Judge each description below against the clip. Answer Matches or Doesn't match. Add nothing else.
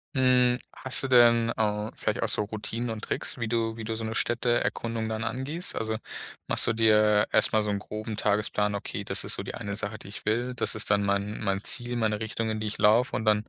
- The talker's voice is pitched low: Matches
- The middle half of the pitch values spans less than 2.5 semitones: Matches